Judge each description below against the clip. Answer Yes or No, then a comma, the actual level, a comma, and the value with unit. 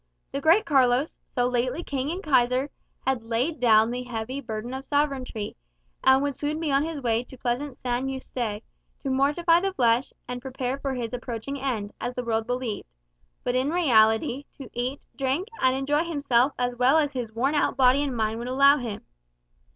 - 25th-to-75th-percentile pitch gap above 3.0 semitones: No, average, 2.7 semitones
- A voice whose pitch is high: Yes, very high, 260 Hz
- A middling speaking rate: Yes, average, 190 wpm